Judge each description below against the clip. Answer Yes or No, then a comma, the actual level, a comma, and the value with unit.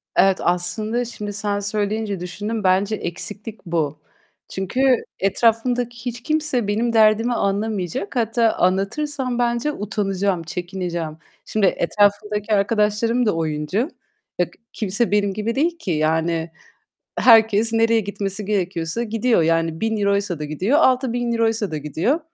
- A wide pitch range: No, average, 3.7 semitones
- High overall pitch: Yes, high, 210 Hz